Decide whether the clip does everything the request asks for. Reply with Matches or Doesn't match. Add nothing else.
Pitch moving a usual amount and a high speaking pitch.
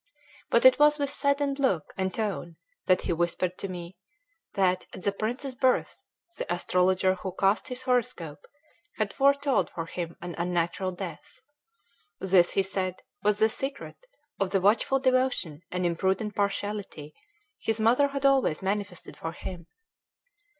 Doesn't match